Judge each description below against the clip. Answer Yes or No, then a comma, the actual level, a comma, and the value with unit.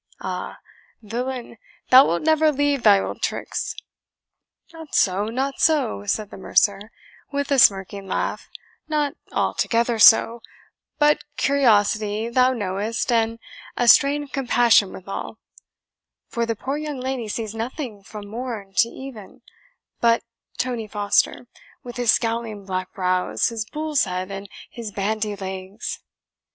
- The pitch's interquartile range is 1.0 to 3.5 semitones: No, average, 4.2 semitones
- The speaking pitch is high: Yes, high, 230 Hz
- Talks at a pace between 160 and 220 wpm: No, slow, 135 wpm